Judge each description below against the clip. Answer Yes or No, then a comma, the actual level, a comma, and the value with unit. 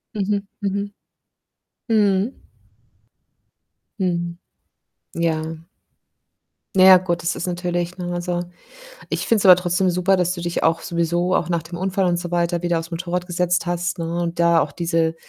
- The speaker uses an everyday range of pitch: No, narrow, 1.3 semitones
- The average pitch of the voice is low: No, medium, 175 Hz